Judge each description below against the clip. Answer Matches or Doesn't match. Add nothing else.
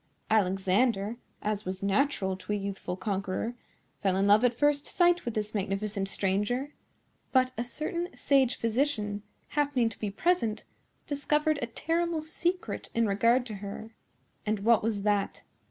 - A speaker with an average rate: Matches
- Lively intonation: Matches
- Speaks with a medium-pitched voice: Doesn't match